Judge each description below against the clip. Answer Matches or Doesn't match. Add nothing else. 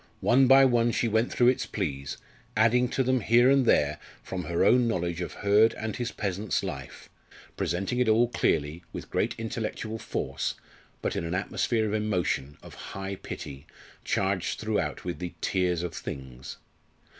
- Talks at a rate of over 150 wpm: Matches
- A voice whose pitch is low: Matches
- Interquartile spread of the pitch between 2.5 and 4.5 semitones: Doesn't match